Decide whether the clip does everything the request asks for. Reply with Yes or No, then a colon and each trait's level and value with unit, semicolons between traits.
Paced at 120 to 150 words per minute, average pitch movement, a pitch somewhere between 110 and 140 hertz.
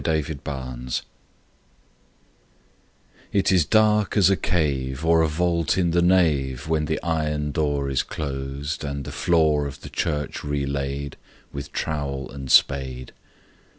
No: average, 140 wpm; average, 3.0 semitones; very low, 75 Hz